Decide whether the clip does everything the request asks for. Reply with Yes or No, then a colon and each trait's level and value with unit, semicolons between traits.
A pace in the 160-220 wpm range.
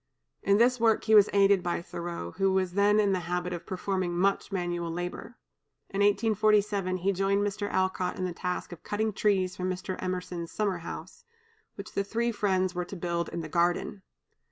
Yes: average, 190 wpm